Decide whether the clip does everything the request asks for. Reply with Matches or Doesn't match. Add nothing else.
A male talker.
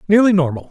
Matches